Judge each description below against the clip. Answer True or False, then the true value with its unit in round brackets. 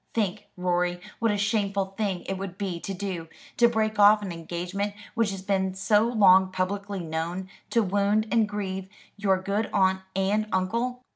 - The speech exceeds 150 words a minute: True (170 wpm)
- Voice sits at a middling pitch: False (195 Hz)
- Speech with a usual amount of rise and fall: False (2.0 semitones)